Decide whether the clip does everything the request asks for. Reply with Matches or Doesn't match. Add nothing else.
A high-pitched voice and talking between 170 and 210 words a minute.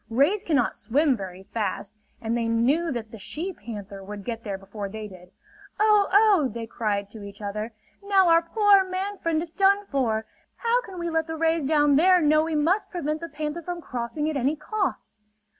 Matches